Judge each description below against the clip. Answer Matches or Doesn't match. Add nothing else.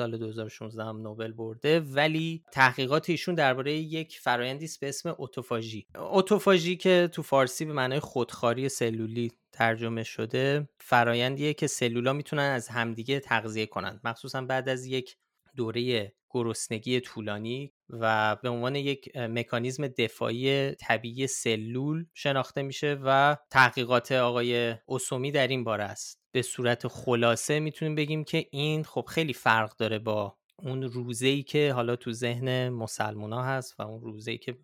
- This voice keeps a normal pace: Matches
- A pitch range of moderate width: Matches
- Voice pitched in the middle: Doesn't match